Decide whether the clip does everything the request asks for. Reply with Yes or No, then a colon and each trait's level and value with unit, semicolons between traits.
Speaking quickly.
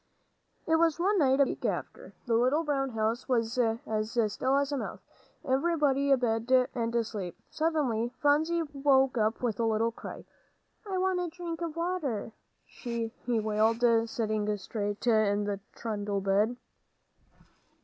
No: average, 150 wpm